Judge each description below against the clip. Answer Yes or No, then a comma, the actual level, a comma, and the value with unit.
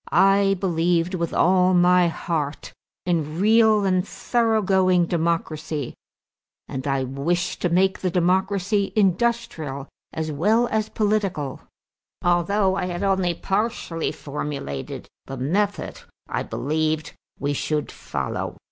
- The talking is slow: Yes, slow, 120 wpm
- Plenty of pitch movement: No, average, 3.9 semitones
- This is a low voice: No, medium, 180 Hz